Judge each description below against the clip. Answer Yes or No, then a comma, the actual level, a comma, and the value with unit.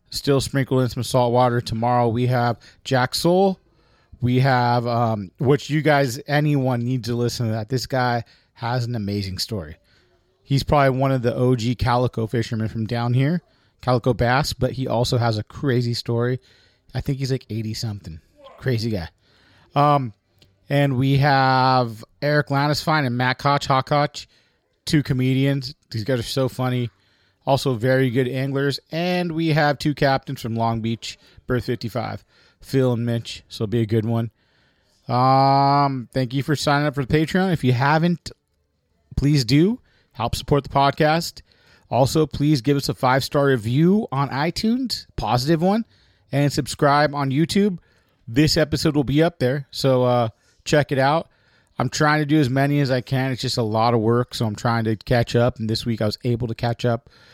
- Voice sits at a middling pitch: No, low, 125 Hz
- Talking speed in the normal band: Yes, average, 180 wpm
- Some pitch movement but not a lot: Yes, average, 3.6 semitones